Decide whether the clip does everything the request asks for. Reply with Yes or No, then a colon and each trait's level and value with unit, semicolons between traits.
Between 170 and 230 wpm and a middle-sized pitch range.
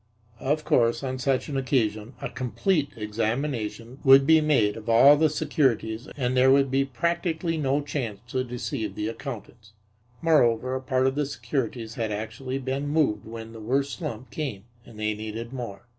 Yes: average, 175 wpm; average, 3.8 semitones